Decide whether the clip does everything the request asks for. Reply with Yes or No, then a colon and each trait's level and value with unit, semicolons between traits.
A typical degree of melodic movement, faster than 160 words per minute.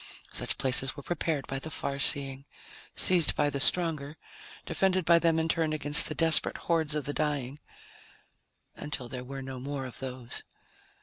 Yes: average, 3.2 semitones; average, 170 wpm